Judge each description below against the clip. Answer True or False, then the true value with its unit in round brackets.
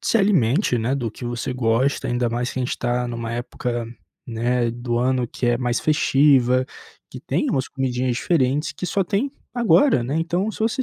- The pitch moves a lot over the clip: False (4.0 semitones)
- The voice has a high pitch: False (125 Hz)